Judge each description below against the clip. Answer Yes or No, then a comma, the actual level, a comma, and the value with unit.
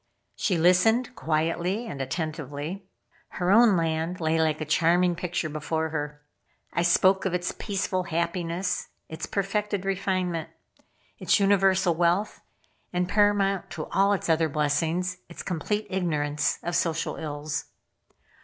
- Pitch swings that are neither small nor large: Yes, average, 3.2 semitones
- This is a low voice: No, medium, 175 Hz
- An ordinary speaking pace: No, slow, 130 wpm